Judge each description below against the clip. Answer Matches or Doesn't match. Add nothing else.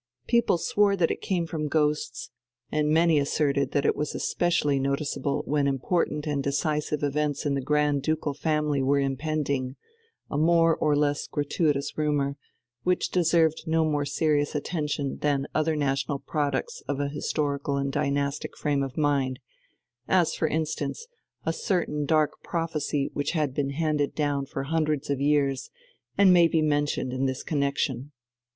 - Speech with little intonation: Matches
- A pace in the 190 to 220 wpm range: Doesn't match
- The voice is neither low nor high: Matches